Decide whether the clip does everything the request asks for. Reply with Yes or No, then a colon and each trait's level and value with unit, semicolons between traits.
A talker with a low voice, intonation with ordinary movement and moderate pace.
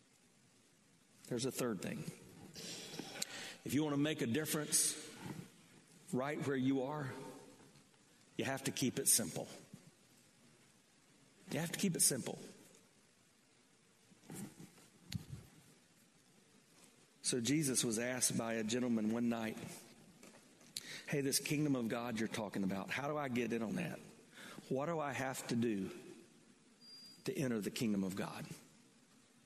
No: low, 130 Hz; average, 3.8 semitones; slow, 130 wpm